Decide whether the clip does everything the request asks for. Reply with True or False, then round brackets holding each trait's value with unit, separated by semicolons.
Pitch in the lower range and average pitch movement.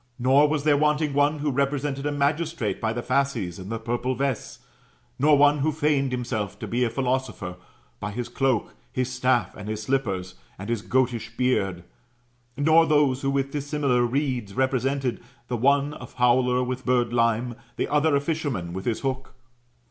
True (130 Hz; 3.3 semitones)